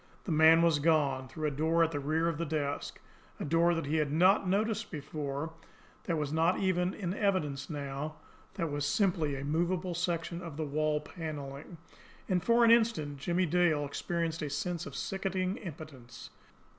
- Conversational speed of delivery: Yes, average, 180 wpm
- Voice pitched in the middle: Yes, medium, 160 Hz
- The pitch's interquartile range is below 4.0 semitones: Yes, average, 3.4 semitones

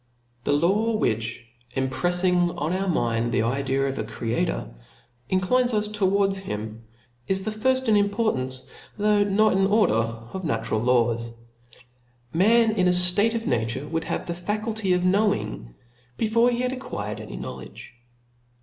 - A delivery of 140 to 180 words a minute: Yes, average, 150 wpm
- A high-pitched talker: No, medium, 180 Hz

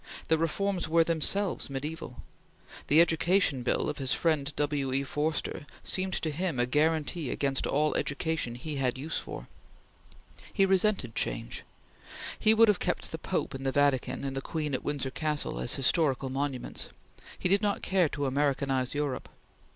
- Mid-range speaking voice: Yes, medium, 150 Hz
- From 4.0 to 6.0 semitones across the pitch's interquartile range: No, average, 3.6 semitones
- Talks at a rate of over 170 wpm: No, average, 165 wpm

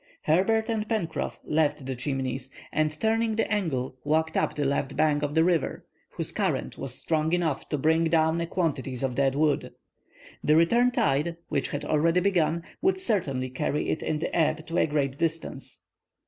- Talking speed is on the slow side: No, average, 180 wpm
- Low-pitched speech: No, medium, 155 Hz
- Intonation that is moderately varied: Yes, average, 3.3 semitones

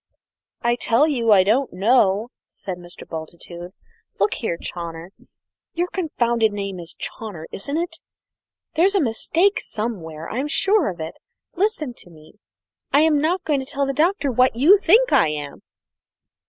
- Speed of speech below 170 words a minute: Yes, average, 155 wpm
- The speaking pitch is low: No, high, 235 Hz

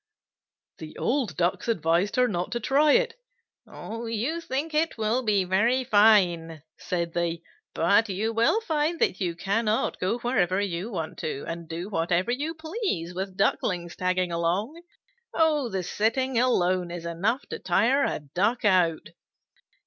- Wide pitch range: Yes, wide, 6.3 semitones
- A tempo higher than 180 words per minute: No, average, 150 wpm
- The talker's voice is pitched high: Yes, high, 205 Hz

